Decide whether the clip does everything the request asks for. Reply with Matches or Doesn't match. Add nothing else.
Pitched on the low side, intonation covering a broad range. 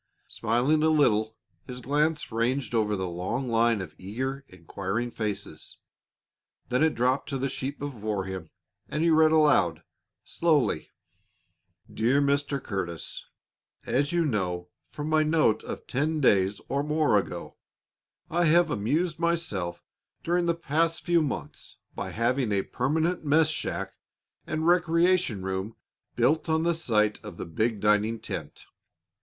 Matches